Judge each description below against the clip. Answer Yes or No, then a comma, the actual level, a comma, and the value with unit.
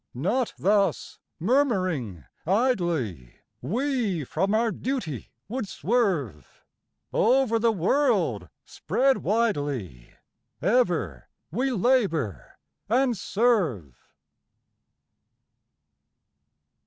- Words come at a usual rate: No, slow, 70 wpm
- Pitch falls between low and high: No, high, 200 Hz